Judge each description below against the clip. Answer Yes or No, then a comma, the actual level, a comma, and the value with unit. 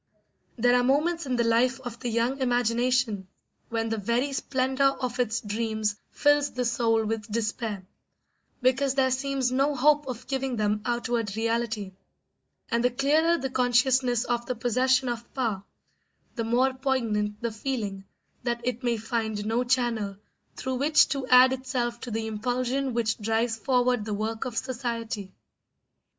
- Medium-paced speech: Yes, average, 155 wpm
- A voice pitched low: No, high, 240 Hz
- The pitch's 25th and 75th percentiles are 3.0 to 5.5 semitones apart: No, narrow, 2.6 semitones